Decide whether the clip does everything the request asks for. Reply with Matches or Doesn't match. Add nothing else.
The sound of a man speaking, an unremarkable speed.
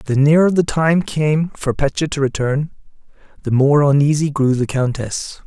Matches